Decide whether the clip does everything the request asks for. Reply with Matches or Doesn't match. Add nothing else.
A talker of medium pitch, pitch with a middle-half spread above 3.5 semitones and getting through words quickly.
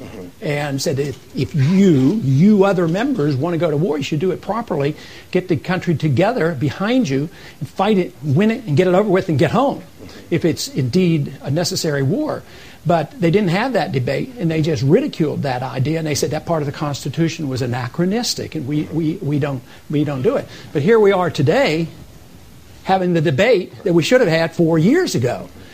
Matches